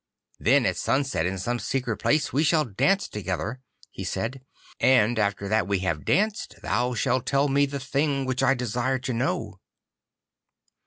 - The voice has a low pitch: Yes, low, 125 Hz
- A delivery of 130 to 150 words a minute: No, average, 165 wpm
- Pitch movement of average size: Yes, average, 4.5 semitones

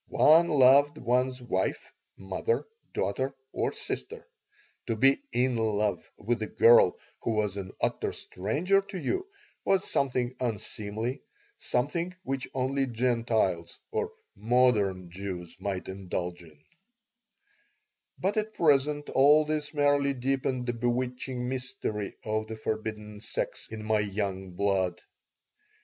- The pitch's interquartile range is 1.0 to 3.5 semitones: No, average, 5.1 semitones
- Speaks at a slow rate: Yes, slow, 125 wpm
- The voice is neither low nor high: No, low, 120 Hz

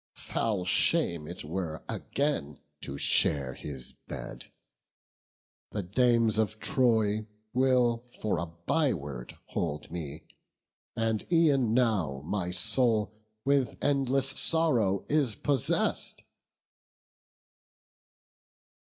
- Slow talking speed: Yes, slow, 90 wpm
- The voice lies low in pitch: Yes, low, 110 Hz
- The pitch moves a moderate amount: No, wide, 7.4 semitones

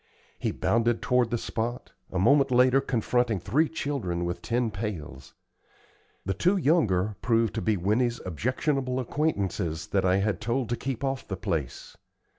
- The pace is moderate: Yes, average, 155 wpm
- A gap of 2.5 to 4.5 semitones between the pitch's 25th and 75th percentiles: No, average, 5.2 semitones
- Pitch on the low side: Yes, low, 115 Hz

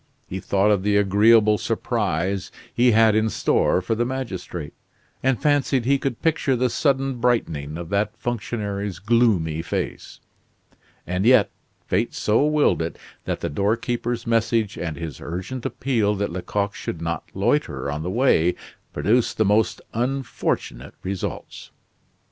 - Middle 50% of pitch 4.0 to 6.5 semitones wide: Yes, average, 4.7 semitones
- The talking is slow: No, average, 145 wpm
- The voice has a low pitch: Yes, low, 105 Hz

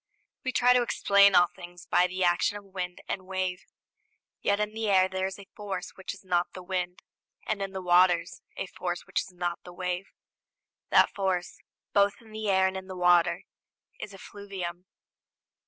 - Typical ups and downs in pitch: No, narrow, 2.0 semitones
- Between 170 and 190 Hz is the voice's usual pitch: Yes, medium, 185 Hz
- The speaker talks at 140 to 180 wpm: No, average, 190 wpm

